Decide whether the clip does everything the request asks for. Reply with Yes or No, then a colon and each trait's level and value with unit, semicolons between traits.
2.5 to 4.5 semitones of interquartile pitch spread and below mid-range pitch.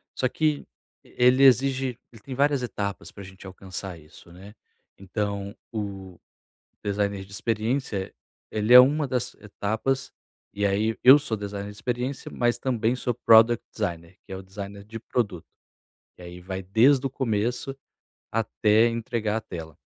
Yes: average, 4.0 semitones; low, 110 Hz